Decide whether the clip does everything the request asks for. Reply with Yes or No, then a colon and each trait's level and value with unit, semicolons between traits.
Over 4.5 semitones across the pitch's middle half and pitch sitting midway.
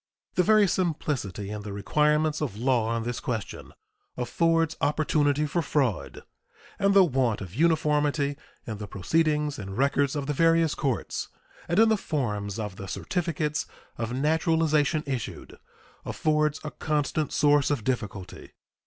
Yes: average, 5.2 semitones; medium, 145 Hz